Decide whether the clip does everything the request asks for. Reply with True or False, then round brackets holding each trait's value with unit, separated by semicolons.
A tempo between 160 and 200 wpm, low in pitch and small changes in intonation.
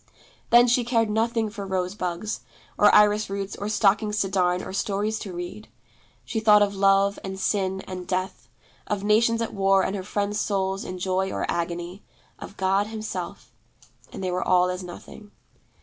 False (180 wpm; 195 Hz; 2.1 semitones)